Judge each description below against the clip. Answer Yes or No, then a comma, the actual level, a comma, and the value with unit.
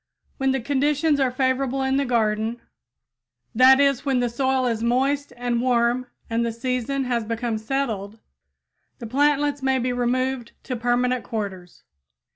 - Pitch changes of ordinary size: No, narrow, 2.3 semitones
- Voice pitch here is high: Yes, very high, 250 Hz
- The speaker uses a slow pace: No, average, 145 wpm